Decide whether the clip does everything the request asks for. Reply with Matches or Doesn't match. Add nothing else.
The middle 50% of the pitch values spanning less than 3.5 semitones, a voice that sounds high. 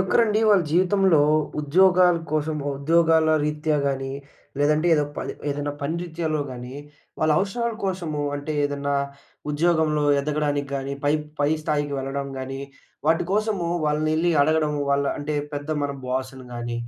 Doesn't match